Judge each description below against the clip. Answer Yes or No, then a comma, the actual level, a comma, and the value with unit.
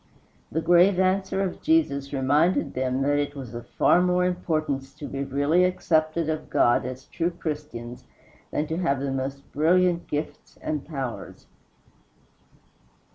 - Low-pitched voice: No, medium, 150 Hz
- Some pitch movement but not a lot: Yes, average, 4.4 semitones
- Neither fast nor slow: Yes, average, 145 wpm